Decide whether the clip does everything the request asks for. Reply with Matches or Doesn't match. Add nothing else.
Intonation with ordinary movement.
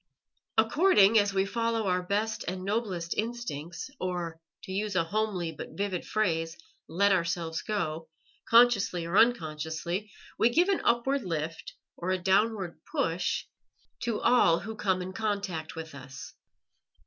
Matches